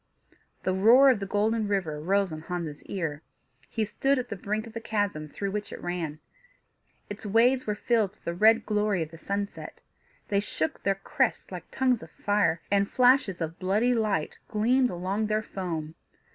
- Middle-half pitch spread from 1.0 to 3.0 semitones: No, average, 3.9 semitones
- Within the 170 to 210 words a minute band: Yes, average, 185 wpm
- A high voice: Yes, high, 205 Hz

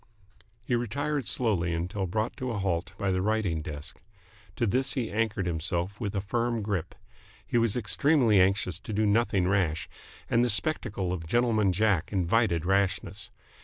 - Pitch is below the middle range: Yes, low, 100 Hz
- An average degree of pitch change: Yes, average, 4.1 semitones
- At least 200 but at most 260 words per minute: No, average, 165 wpm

